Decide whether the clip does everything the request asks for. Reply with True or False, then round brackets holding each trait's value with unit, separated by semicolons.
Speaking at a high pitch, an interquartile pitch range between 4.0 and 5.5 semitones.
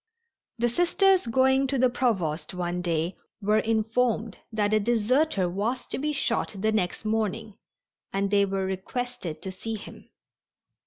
True (220 Hz; 4.4 semitones)